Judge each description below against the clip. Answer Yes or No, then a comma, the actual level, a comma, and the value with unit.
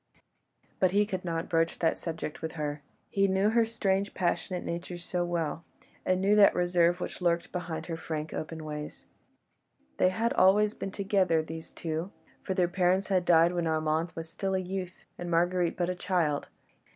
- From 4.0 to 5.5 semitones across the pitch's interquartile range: No, narrow, 2.5 semitones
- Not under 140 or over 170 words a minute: No, average, 180 wpm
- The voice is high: No, medium, 175 Hz